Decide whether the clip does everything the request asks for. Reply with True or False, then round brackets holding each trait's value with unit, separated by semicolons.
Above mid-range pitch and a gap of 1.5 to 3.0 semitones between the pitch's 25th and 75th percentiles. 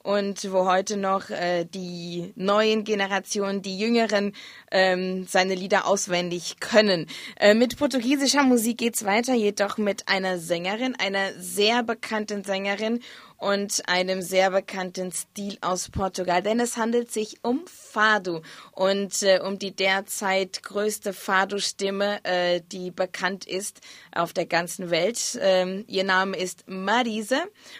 True (195 Hz; 2.4 semitones)